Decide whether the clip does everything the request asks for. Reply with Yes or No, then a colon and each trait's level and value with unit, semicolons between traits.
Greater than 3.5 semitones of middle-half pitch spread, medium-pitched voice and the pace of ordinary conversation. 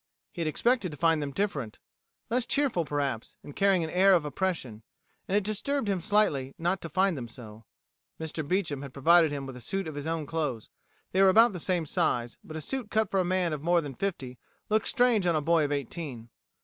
No: wide, 5.4 semitones; medium, 165 Hz; fast, 225 wpm